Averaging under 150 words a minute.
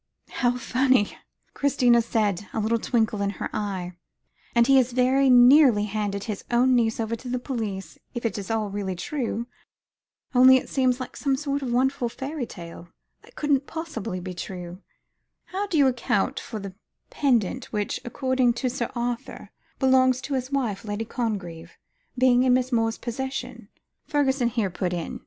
No: average, 165 wpm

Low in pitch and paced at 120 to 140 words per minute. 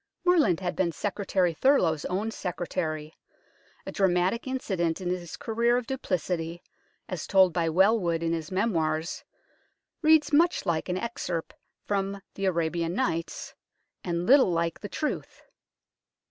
No: medium, 180 Hz; slow, 135 wpm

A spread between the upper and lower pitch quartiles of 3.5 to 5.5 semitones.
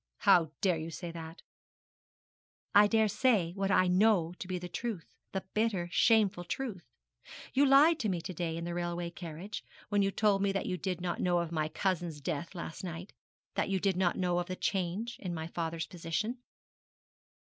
No: average, 3.1 semitones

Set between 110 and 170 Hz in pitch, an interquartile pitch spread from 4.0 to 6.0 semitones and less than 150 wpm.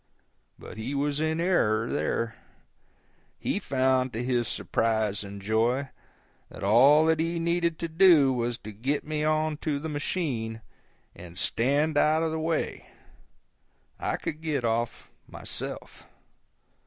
Yes: medium, 140 Hz; wide, 5.5 semitones; average, 140 wpm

